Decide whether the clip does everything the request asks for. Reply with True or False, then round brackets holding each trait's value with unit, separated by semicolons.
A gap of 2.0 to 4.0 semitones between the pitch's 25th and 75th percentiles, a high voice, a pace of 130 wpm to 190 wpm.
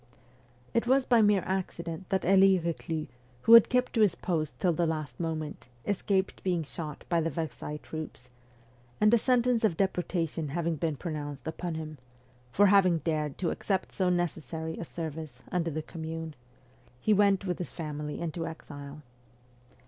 False (3.4 semitones; 165 Hz; 165 wpm)